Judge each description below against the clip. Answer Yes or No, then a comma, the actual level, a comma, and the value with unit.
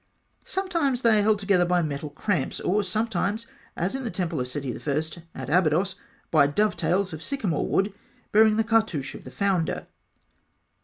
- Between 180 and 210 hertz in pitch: Yes, medium, 185 Hz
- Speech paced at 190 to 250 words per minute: No, average, 165 wpm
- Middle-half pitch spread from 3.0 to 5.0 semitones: No, wide, 5.5 semitones